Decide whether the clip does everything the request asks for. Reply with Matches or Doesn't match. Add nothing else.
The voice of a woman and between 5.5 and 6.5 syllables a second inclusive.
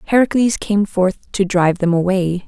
Doesn't match